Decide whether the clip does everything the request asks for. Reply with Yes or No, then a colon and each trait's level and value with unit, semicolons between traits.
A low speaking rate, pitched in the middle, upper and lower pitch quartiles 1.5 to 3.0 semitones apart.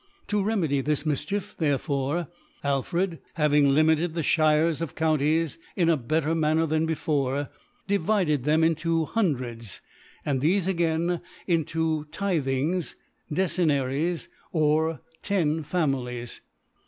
Yes: slow, 120 wpm; medium, 155 Hz; average, 2.7 semitones